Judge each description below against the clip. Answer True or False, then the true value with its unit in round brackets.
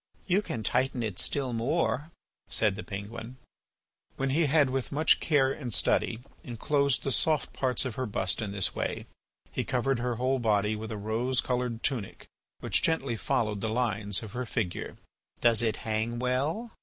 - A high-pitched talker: False (120 Hz)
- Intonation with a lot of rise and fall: False (3.6 semitones)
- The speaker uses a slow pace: False (175 wpm)